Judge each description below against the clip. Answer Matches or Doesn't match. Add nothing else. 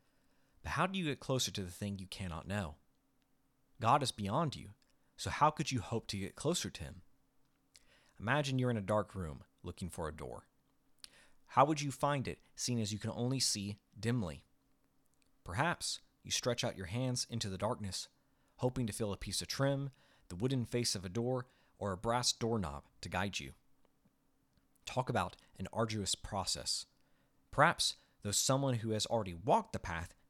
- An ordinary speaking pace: Matches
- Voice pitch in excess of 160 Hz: Doesn't match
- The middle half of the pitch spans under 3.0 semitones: Doesn't match